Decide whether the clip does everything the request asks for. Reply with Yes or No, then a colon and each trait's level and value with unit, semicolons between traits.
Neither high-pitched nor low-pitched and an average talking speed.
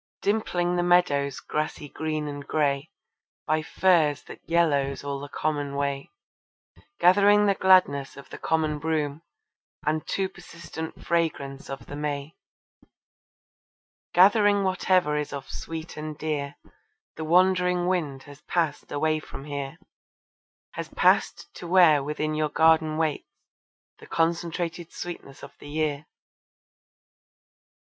No: medium, 155 Hz; slow, 125 wpm